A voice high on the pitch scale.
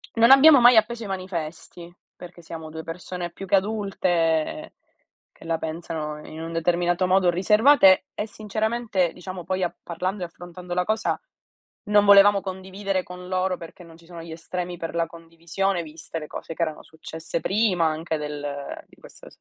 No: medium, 180 Hz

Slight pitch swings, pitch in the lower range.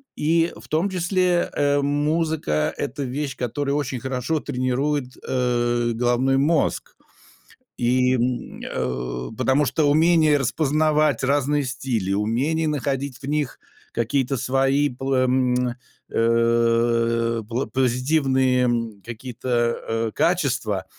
No: average, 3.4 semitones; low, 130 Hz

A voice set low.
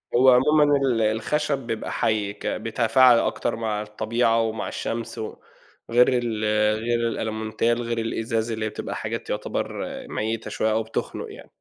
Yes: low, 115 Hz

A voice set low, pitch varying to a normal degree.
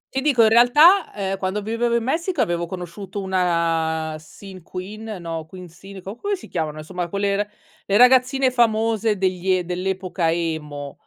No: high, 190 Hz; average, 4.8 semitones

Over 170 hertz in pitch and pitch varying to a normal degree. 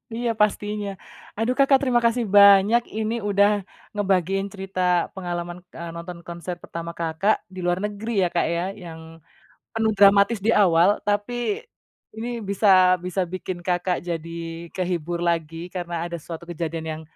Yes: medium, 185 Hz; average, 3.3 semitones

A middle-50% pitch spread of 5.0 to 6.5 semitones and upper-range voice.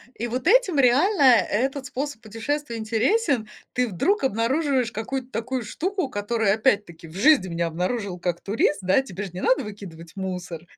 Yes: wide, 5.5 semitones; high, 230 Hz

